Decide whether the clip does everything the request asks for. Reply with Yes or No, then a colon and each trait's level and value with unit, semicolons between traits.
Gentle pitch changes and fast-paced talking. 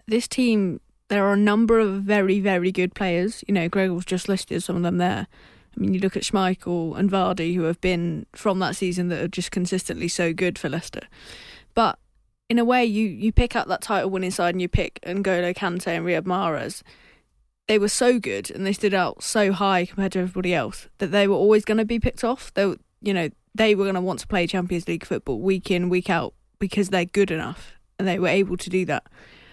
Yes: narrow, 2.2 semitones; fast, 230 wpm